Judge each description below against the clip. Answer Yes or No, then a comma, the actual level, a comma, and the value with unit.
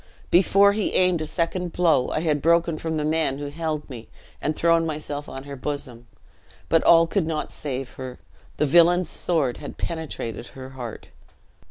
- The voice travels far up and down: No, average, 3.5 semitones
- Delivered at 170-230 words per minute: Yes, average, 175 wpm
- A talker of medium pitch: Yes, medium, 155 Hz